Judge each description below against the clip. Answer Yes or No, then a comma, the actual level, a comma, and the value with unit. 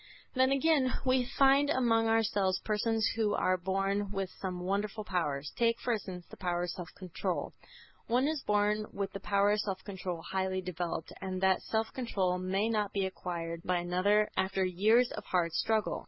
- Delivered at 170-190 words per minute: Yes, average, 180 wpm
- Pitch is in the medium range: No, high, 200 Hz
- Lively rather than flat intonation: No, average, 3.3 semitones